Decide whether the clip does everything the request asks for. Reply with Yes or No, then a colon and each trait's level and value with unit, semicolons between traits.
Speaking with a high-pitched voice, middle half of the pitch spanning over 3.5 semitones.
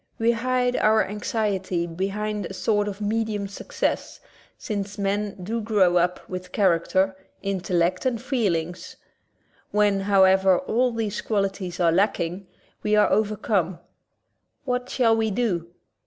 No: high, 200 Hz; average, 2.8 semitones